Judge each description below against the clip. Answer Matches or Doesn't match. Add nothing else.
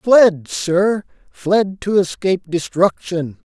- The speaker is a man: Matches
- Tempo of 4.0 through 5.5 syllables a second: Doesn't match